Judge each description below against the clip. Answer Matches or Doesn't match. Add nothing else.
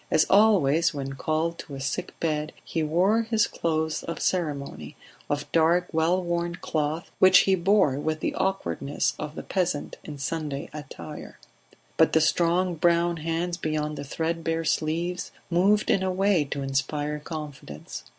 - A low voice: Doesn't match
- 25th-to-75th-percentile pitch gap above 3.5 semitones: Doesn't match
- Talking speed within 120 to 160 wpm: Matches